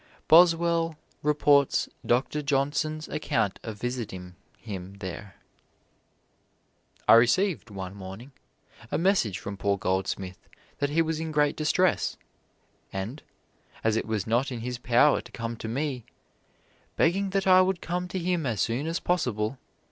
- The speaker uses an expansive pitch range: Yes, wide, 7.2 semitones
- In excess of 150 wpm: No, average, 140 wpm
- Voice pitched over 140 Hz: No, low, 135 Hz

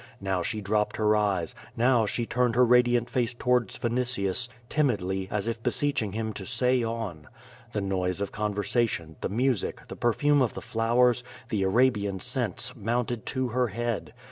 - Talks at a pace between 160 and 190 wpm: Yes, average, 170 wpm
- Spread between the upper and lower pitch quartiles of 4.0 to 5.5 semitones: No, average, 3.5 semitones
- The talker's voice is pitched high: No, low, 115 Hz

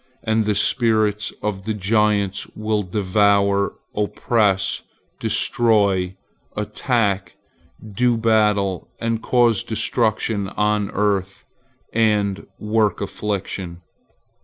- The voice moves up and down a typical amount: No, narrow, 1.8 semitones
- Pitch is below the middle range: Yes, low, 105 Hz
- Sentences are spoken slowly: Yes, slow, 90 wpm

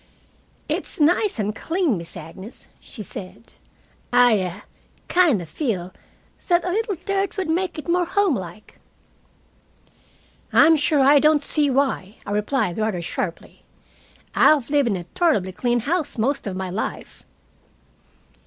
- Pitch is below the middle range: No, very high, 265 Hz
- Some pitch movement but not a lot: No, wide, 8.7 semitones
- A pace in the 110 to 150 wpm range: Yes, average, 140 wpm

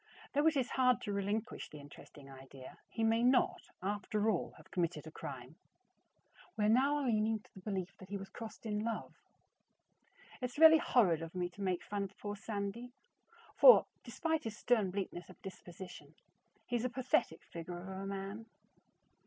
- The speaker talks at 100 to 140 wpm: No, average, 175 wpm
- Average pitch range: Yes, average, 4.1 semitones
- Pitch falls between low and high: No, high, 205 Hz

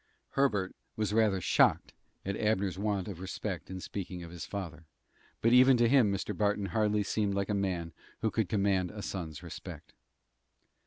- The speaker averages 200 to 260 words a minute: No, average, 170 wpm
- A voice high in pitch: No, low, 100 Hz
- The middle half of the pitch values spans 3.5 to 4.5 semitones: No, narrow, 2.5 semitones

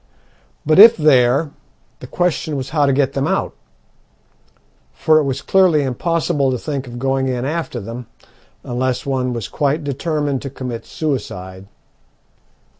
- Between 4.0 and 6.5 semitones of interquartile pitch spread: No, average, 3.4 semitones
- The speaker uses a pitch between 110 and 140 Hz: Yes, low, 135 Hz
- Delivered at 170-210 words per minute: No, average, 145 wpm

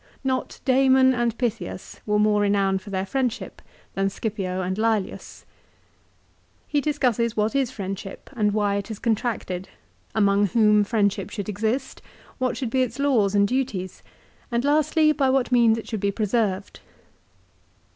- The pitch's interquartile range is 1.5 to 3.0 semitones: No, average, 4.1 semitones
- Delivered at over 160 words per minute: No, average, 150 wpm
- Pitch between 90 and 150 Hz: No, high, 220 Hz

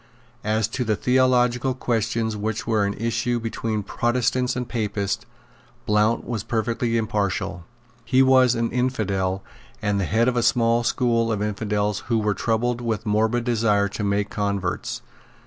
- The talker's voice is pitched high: No, low, 115 Hz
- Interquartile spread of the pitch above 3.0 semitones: No, narrow, 2.5 semitones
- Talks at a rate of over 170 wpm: No, average, 155 wpm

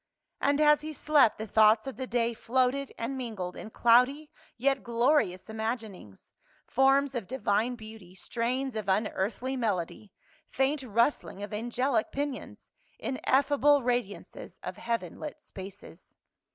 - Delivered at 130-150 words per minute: Yes, slow, 135 wpm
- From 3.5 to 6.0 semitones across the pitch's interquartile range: Yes, average, 3.9 semitones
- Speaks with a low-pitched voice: No, high, 240 Hz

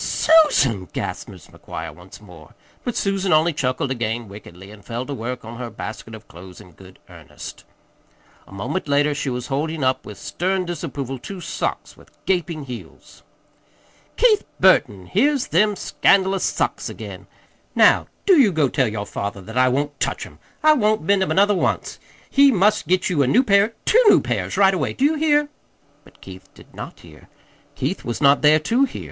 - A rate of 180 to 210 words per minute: Yes, average, 185 wpm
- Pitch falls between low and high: Yes, medium, 145 Hz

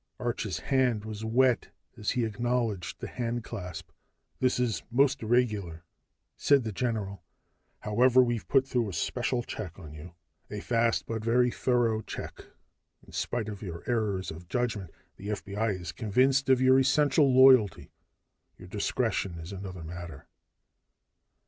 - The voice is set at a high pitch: No, low, 115 Hz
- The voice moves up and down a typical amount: Yes, average, 4.1 semitones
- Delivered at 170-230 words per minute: No, average, 140 wpm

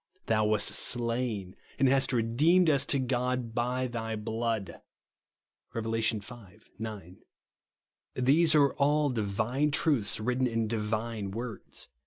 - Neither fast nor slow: No, slow, 120 wpm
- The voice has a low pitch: Yes, low, 120 Hz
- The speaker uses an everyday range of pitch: Yes, average, 3.2 semitones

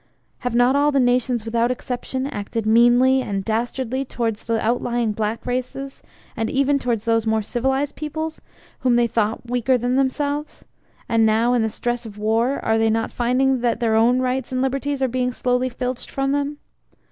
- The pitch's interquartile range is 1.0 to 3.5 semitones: Yes, narrow, 2.6 semitones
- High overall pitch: Yes, high, 245 Hz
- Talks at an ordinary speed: Yes, average, 185 wpm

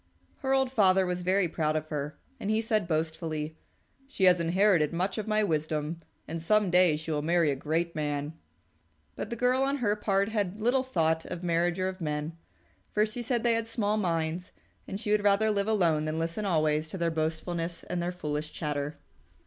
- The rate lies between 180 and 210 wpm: Yes, average, 200 wpm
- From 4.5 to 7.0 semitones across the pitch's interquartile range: Yes, average, 4.8 semitones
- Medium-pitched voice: Yes, medium, 175 Hz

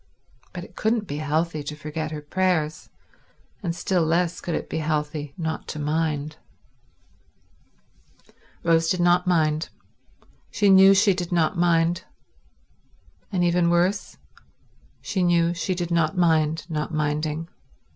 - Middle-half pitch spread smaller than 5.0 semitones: Yes, narrow, 2.5 semitones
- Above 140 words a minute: No, slow, 135 wpm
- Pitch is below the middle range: No, medium, 165 Hz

